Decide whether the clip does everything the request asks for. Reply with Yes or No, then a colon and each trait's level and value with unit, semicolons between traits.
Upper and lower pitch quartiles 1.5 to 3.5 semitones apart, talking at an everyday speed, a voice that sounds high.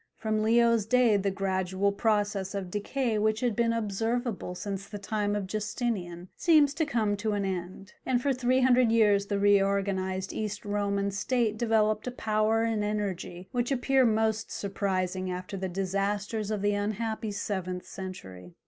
Yes: narrow, 2.5 semitones; average, 160 wpm; high, 205 Hz